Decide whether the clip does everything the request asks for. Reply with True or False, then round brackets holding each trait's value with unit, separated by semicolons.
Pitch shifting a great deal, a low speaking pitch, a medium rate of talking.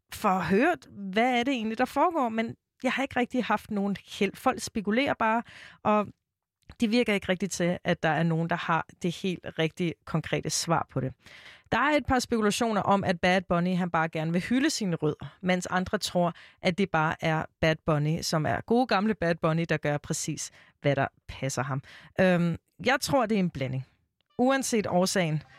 False (5.8 semitones; 180 Hz; 200 wpm)